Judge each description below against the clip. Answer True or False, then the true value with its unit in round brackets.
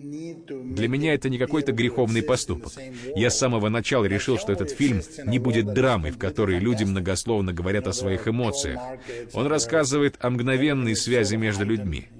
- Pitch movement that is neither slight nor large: True (4.0 semitones)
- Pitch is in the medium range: False (120 Hz)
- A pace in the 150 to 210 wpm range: True (160 wpm)